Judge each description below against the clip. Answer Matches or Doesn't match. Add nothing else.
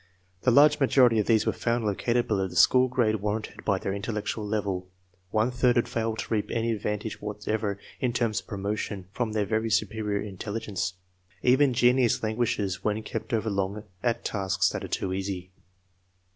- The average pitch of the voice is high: Doesn't match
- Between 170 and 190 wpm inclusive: Matches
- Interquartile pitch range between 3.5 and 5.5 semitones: Doesn't match